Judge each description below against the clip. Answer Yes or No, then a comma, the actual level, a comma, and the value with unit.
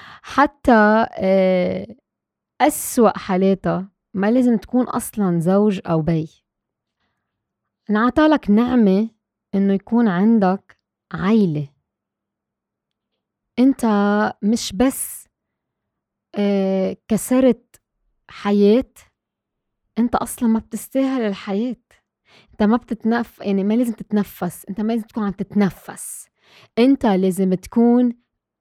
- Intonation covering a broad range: No, average, 3.5 semitones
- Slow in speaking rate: No, average, 90 wpm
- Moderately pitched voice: No, high, 210 Hz